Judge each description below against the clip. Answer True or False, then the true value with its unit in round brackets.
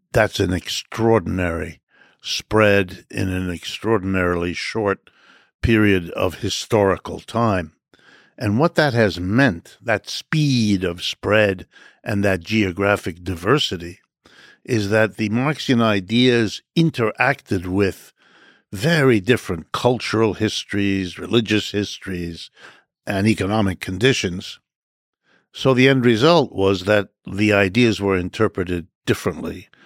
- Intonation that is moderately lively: True (3.4 semitones)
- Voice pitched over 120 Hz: False (105 Hz)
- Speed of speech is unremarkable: False (105 wpm)